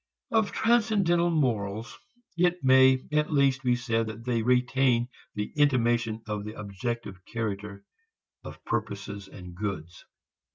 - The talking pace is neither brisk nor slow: No, slow, 125 wpm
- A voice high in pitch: No, low, 120 Hz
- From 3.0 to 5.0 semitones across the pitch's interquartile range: Yes, average, 4.5 semitones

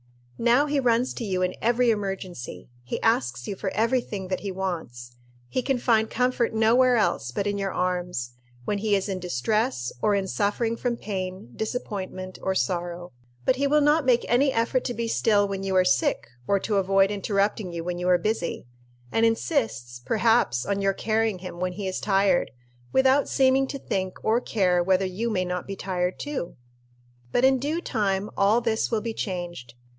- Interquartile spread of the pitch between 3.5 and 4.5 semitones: Yes, average, 4.1 semitones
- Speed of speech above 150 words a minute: Yes, average, 190 wpm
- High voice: Yes, high, 200 Hz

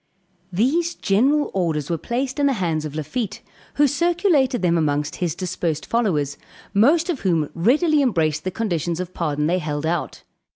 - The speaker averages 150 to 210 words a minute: Yes, average, 165 wpm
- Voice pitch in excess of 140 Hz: Yes, medium, 185 Hz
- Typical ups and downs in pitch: No, wide, 8.8 semitones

